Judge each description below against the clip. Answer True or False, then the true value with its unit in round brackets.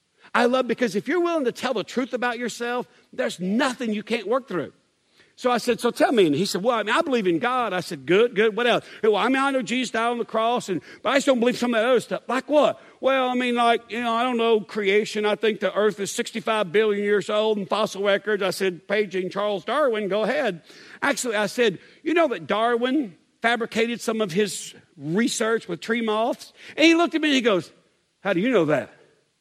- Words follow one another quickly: True (250 wpm)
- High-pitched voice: True (230 Hz)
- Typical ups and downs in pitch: True (3.0 semitones)